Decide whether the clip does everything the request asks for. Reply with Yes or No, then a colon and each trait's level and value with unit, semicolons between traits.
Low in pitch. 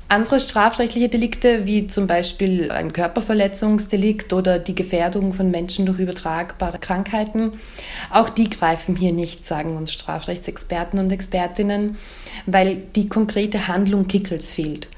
No: high, 190 Hz